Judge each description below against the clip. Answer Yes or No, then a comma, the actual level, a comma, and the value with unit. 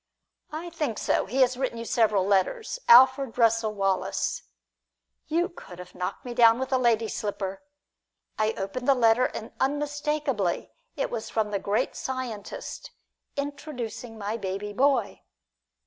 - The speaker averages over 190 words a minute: No, average, 145 wpm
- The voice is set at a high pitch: Yes, high, 235 Hz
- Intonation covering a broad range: No, average, 4.5 semitones